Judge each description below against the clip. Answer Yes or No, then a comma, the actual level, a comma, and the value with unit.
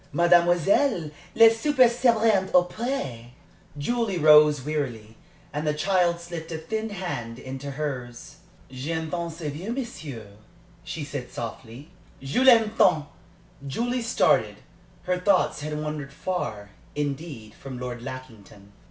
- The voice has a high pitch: No, medium, 155 Hz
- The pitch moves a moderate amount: No, wide, 6.2 semitones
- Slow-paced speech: Yes, slow, 125 wpm